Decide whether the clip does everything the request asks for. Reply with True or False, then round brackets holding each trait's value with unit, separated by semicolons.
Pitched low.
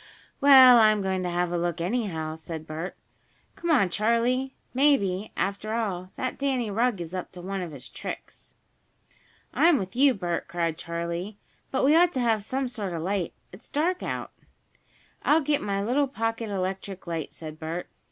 False (200 Hz)